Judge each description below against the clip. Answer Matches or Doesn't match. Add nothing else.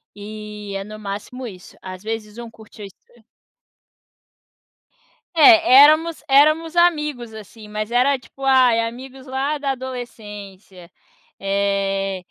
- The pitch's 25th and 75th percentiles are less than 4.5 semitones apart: Doesn't match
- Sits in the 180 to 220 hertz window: Doesn't match